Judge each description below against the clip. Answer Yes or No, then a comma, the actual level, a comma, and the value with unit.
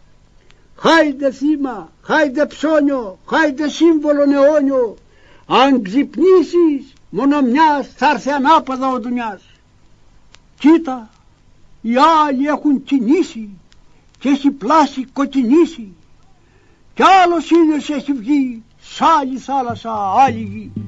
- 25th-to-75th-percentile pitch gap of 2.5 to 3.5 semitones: Yes, average, 2.9 semitones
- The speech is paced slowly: Yes, slow, 100 wpm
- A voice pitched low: No, very high, 280 Hz